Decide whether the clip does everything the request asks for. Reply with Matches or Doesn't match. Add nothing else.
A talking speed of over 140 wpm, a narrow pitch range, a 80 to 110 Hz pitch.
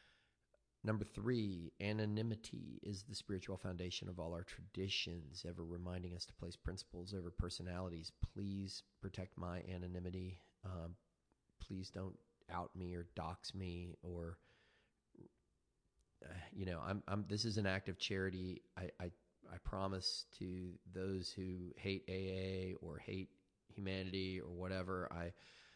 Doesn't match